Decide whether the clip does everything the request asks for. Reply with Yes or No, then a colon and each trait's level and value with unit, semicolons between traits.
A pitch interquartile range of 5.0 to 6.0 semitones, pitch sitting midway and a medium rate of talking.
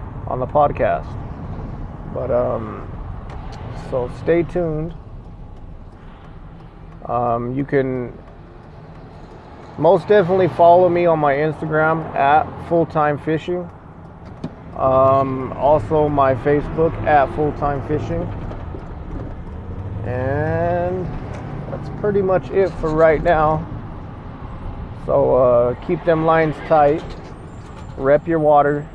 No: average, 5.3 semitones; medium, 145 Hz; slow, 95 wpm